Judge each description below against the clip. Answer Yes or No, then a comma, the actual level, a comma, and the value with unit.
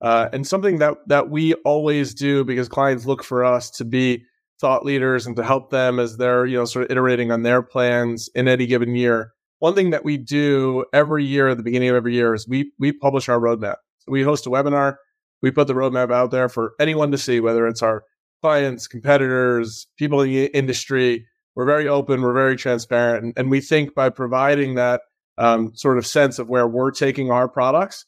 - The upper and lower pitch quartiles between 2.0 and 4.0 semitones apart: Yes, narrow, 2.4 semitones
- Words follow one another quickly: Yes, fast, 215 wpm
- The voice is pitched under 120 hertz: No, low, 130 Hz